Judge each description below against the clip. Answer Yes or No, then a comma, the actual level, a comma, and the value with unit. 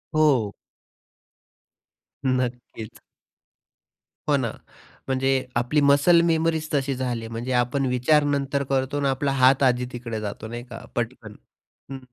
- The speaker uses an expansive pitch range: No, average, 2.7 semitones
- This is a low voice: Yes, low, 130 Hz